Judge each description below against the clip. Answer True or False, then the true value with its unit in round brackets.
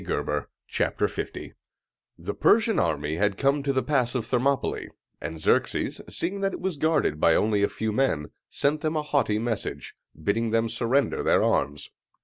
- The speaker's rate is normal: True (170 wpm)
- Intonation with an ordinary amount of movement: False (6.1 semitones)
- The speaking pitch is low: True (120 Hz)